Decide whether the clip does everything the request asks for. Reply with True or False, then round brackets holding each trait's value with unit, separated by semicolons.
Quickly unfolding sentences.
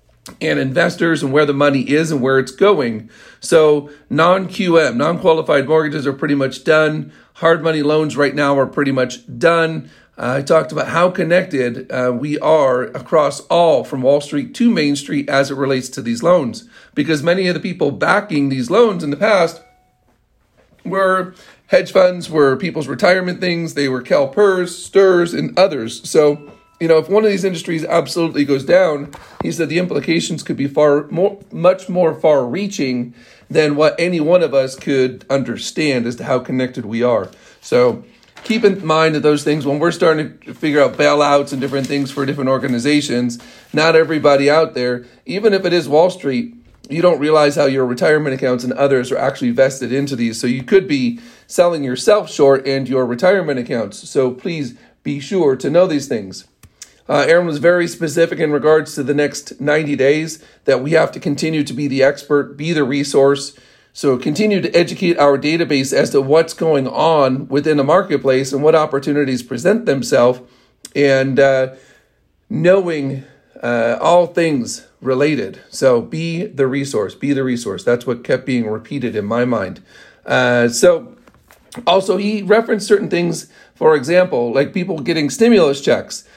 False (180 wpm)